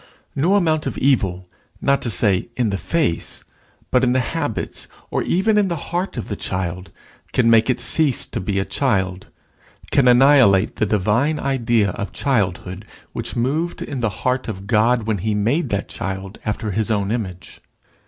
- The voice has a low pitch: Yes, low, 115 Hz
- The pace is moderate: Yes, average, 175 wpm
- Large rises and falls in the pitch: Yes, wide, 5.7 semitones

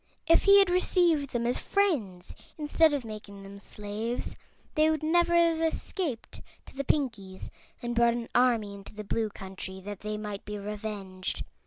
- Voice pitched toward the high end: Yes, high, 230 Hz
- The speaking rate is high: No, average, 170 wpm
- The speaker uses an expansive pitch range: Yes, wide, 7.3 semitones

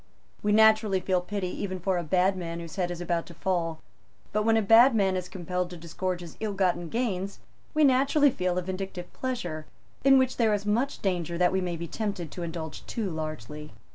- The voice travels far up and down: No, average, 3.5 semitones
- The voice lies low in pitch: No, medium, 185 Hz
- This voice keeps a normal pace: No, fast, 210 wpm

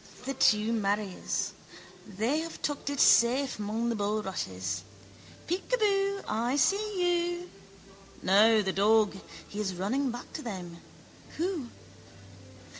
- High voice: Yes, high, 230 Hz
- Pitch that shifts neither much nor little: No, wide, 7.7 semitones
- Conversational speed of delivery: No, slow, 115 wpm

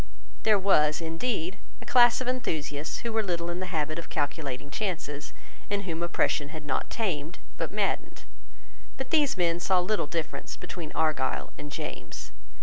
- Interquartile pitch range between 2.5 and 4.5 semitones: No, average, 5.0 semitones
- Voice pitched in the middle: Yes, medium, 170 Hz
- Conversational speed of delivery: Yes, average, 160 wpm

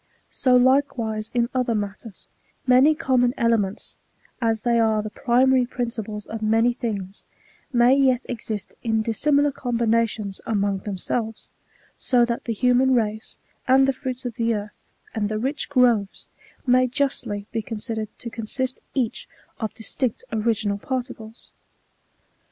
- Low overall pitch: No, high, 235 Hz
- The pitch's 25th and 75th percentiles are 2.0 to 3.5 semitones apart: Yes, average, 2.7 semitones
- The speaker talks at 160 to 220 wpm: No, average, 140 wpm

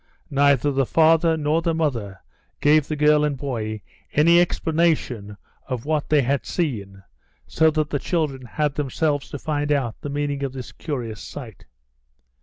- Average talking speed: Yes, average, 160 wpm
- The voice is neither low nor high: Yes, medium, 145 Hz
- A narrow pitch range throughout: No, average, 3.4 semitones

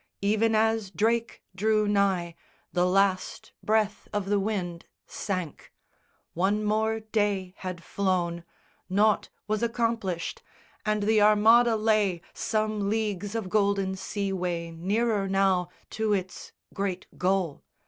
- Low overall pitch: No, high, 200 Hz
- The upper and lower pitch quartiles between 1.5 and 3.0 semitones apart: Yes, narrow, 2.6 semitones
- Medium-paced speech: No, slow, 120 wpm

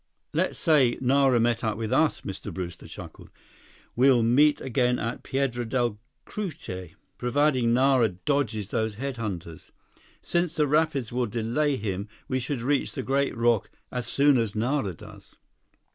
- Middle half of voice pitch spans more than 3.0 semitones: Yes, average, 3.9 semitones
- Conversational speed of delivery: Yes, average, 155 wpm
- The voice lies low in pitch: Yes, low, 125 Hz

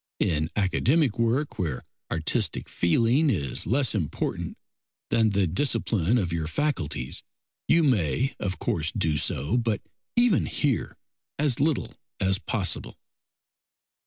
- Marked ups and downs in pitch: Yes, wide, 8.3 semitones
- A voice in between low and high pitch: No, low, 105 Hz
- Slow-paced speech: Yes, slow, 120 wpm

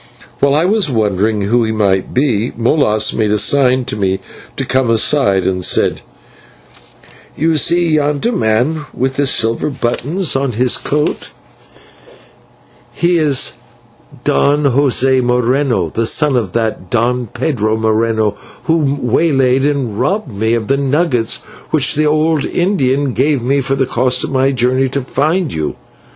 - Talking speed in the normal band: Yes, average, 150 wpm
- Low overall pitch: Yes, low, 130 Hz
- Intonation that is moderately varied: Yes, average, 4.3 semitones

